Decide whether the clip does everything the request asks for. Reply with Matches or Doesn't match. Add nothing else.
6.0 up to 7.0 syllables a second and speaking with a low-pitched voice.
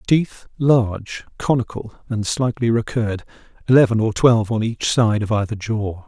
Doesn't match